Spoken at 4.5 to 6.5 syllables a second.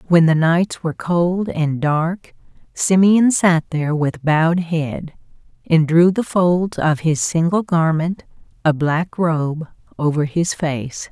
No: 3.6 syllables/s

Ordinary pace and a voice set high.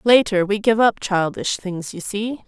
Yes: average, 195 wpm; high, 205 Hz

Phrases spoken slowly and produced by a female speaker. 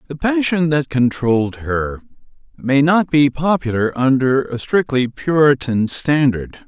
No: slow, 125 wpm; male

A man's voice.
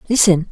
No: female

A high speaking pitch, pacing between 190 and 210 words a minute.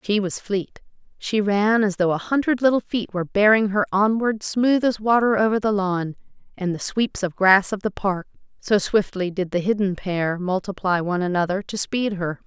Yes: high, 200 Hz; average, 195 wpm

